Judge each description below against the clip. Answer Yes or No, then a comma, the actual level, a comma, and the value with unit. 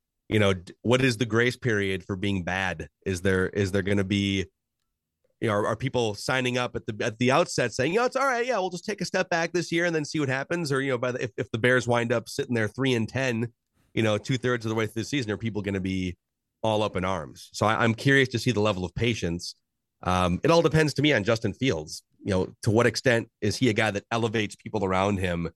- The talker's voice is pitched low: Yes, low, 115 Hz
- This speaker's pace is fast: Yes, fast, 275 wpm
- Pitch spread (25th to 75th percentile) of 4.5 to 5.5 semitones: Yes, average, 4.8 semitones